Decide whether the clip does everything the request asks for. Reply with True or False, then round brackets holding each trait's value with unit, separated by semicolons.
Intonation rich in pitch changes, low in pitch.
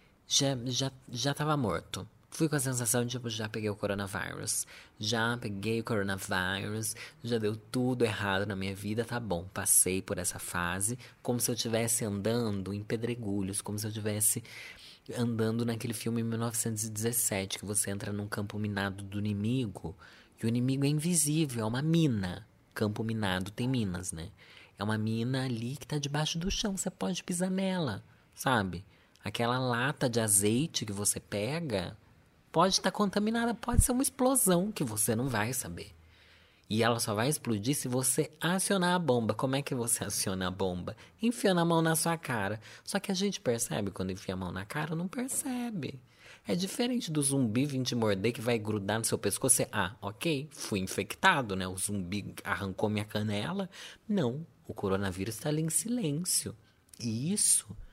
True (6.3 semitones; 115 Hz)